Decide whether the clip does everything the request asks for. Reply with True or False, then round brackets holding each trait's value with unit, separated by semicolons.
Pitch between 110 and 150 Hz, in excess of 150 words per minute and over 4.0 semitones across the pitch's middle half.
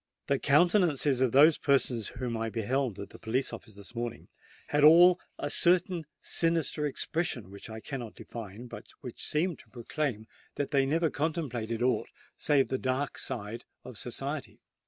True (135 Hz; 160 wpm; 4.6 semitones)